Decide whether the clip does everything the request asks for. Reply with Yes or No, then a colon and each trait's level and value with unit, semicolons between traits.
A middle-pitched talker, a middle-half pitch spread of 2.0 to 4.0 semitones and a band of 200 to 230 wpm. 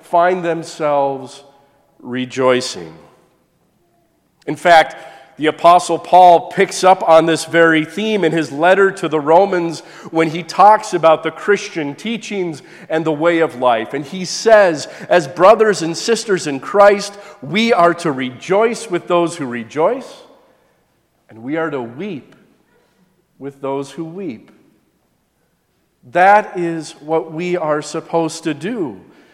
No: medium, 165 Hz; average, 3.2 semitones; slow, 135 wpm